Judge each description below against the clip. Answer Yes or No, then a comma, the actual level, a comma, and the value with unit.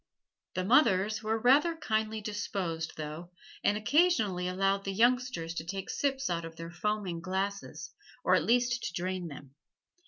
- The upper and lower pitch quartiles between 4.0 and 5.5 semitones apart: Yes, average, 4.8 semitones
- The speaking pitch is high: Yes, high, 200 Hz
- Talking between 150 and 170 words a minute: Yes, average, 155 wpm